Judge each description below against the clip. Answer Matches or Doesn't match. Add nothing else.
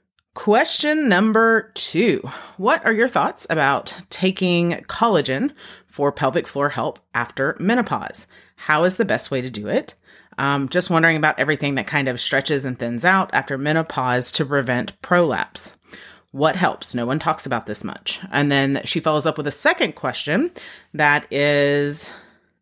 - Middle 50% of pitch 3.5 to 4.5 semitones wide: Matches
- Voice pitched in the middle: Matches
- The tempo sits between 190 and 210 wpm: Doesn't match